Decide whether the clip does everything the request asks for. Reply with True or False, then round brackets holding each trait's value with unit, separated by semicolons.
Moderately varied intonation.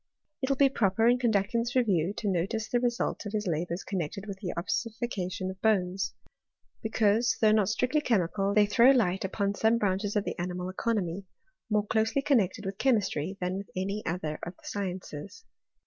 True (3.3 semitones)